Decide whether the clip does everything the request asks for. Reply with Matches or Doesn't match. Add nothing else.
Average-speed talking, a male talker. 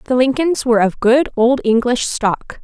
Doesn't match